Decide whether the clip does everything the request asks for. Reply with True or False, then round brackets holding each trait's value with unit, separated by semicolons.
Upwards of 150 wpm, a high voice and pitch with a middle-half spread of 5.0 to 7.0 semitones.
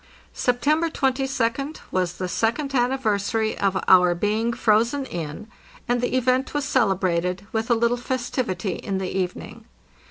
False (135 wpm; 230 Hz; 5.3 semitones)